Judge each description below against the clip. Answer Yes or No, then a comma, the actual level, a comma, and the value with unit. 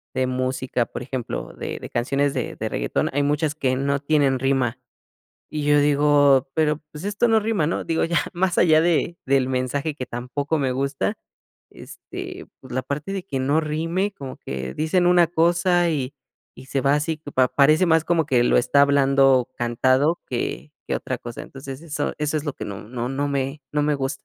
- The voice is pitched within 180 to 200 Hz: No, medium, 140 Hz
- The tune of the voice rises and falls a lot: No, average, 3.2 semitones